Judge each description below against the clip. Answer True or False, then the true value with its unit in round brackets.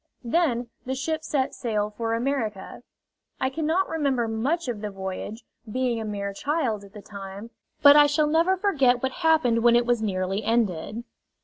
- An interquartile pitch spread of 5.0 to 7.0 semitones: True (5.5 semitones)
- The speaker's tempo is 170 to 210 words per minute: True (175 wpm)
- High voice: True (240 Hz)